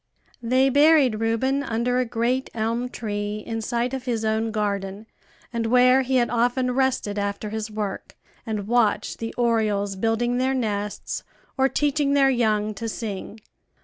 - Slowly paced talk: No, average, 155 wpm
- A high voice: Yes, high, 230 Hz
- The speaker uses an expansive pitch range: No, average, 2.9 semitones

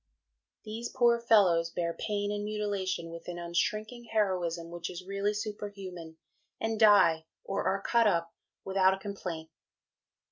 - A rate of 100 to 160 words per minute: Yes, average, 140 wpm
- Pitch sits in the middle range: No, high, 195 Hz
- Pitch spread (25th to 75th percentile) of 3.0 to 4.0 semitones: Yes, average, 3.6 semitones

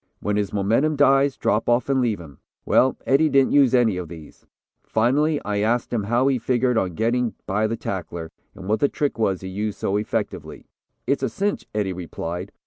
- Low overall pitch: Yes, low, 110 Hz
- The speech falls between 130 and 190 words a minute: No, average, 200 wpm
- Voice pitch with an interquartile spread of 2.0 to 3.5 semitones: No, average, 5.1 semitones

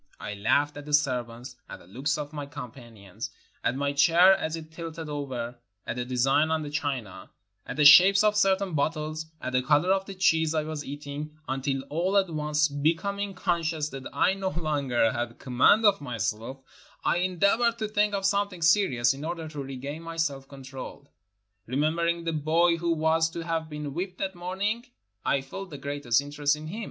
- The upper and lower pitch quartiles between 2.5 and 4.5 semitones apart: Yes, average, 4.0 semitones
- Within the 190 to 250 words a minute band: Yes, average, 195 wpm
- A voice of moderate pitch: Yes, medium, 155 Hz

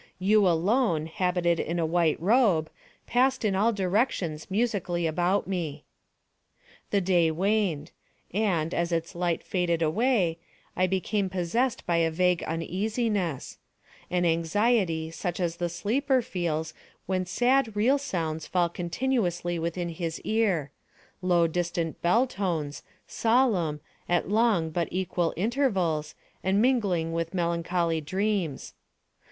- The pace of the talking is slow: Yes, slow, 120 wpm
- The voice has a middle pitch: Yes, medium, 180 Hz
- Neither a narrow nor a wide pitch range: Yes, average, 3.9 semitones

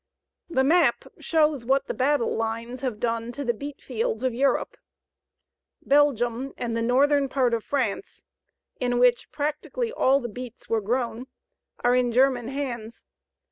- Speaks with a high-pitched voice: Yes, very high, 250 Hz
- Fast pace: No, average, 145 wpm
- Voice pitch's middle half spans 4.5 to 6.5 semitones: No, average, 3.0 semitones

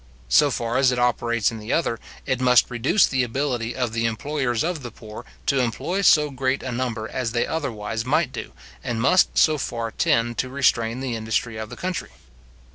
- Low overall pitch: Yes, low, 125 Hz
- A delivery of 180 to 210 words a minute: Yes, average, 200 wpm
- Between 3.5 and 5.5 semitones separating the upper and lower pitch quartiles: No, average, 3.1 semitones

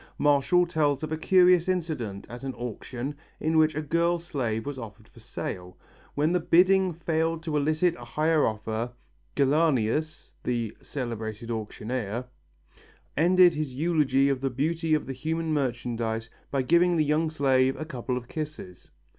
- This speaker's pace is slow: No, average, 155 wpm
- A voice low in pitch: No, medium, 145 Hz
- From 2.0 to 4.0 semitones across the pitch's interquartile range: No, average, 4.9 semitones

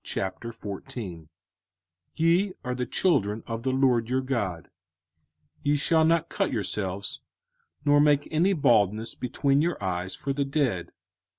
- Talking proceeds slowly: Yes, slow, 130 wpm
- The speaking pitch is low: Yes, low, 130 Hz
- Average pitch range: No, wide, 6.1 semitones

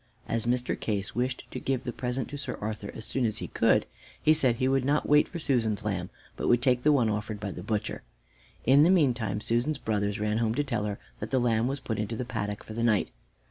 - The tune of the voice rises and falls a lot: No, average, 3.7 semitones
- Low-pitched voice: Yes, low, 120 Hz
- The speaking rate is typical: No, fast, 245 wpm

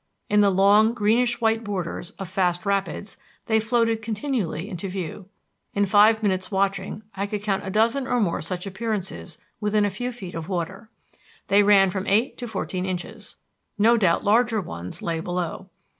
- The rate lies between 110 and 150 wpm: No, average, 175 wpm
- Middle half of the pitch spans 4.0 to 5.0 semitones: No, average, 2.9 semitones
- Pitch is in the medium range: No, high, 200 Hz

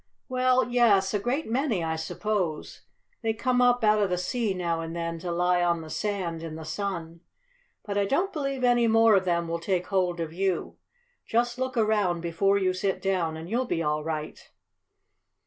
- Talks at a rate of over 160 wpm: Yes, average, 195 wpm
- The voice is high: Yes, high, 195 Hz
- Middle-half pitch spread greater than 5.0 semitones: Yes, wide, 5.4 semitones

